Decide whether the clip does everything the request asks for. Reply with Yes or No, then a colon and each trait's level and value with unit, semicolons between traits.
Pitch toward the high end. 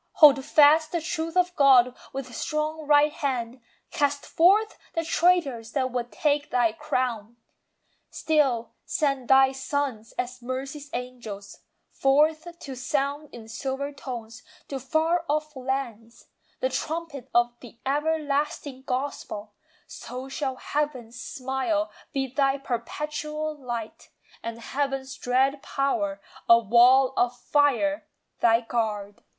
Yes: very high, 270 Hz